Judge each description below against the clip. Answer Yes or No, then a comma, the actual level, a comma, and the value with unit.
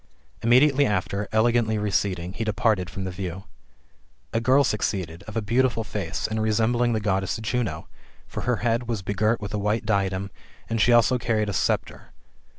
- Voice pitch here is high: No, low, 110 Hz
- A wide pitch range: No, average, 3.0 semitones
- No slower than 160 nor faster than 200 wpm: Yes, average, 175 wpm